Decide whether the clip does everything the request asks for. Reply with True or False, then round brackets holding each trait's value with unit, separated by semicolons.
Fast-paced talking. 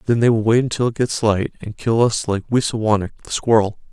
True (230 wpm)